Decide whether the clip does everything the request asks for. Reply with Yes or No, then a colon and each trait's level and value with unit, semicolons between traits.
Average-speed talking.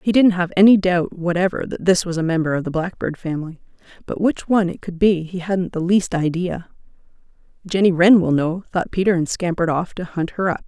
No: fast, 220 wpm